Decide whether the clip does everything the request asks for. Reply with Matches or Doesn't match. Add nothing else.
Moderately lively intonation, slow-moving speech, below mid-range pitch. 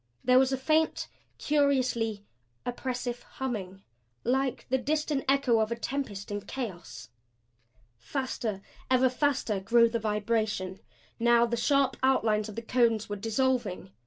Doesn't match